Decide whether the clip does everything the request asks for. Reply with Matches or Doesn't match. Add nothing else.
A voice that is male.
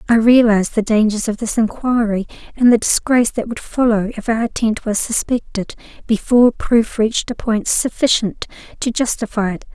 Doesn't match